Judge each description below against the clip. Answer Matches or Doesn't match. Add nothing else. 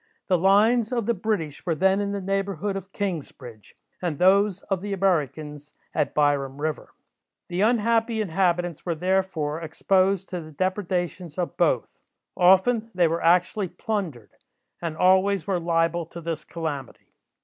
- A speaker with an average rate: Matches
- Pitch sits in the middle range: Matches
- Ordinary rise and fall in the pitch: Matches